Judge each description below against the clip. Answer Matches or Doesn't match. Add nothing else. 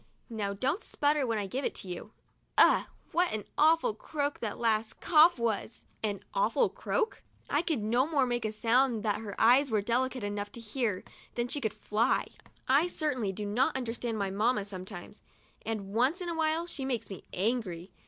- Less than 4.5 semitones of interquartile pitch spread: Doesn't match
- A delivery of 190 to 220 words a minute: Matches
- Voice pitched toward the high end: Matches